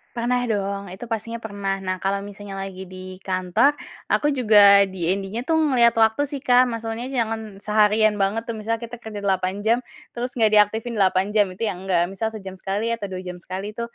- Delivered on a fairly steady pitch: No, average, 3.0 semitones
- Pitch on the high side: Yes, high, 210 Hz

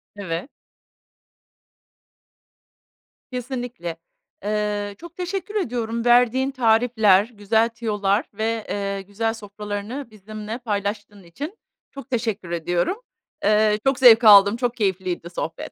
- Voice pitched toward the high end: Yes, high, 220 Hz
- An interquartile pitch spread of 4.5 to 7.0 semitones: No, average, 3.2 semitones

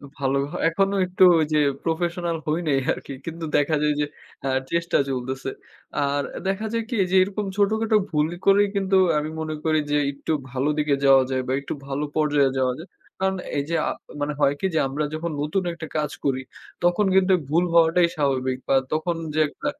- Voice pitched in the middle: Yes, medium, 155 Hz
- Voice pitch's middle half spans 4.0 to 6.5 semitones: Yes, average, 4.3 semitones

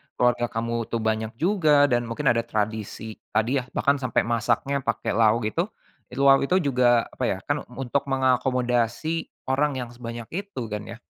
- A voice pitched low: Yes, low, 120 Hz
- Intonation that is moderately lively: Yes, average, 3.1 semitones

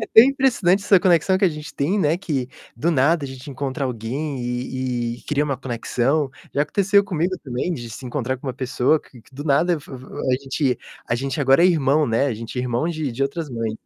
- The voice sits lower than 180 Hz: Yes, medium, 140 Hz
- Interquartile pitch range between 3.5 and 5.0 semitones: Yes, average, 4.5 semitones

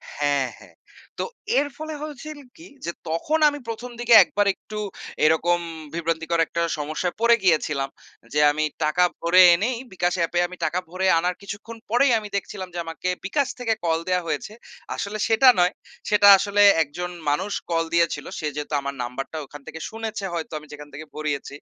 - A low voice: No, medium, 175 Hz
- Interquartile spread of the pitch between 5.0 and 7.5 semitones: Yes, wide, 5.4 semitones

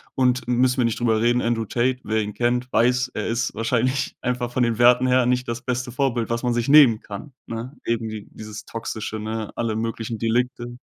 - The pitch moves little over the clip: Yes, narrow, 1.8 semitones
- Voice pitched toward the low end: Yes, low, 120 Hz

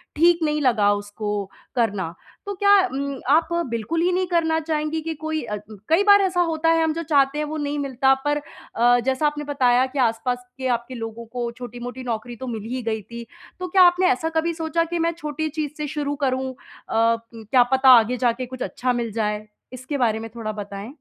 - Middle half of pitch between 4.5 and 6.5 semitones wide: Yes, average, 5.3 semitones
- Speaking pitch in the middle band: No, very high, 260 Hz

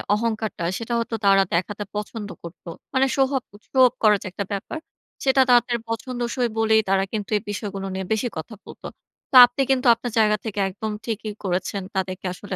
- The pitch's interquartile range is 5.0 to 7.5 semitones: No, average, 3.4 semitones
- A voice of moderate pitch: No, high, 220 Hz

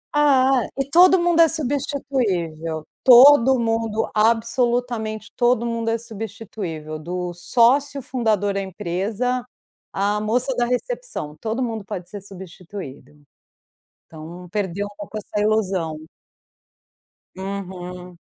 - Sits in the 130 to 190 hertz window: No, high, 215 Hz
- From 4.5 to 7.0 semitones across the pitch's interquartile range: Yes, average, 5.2 semitones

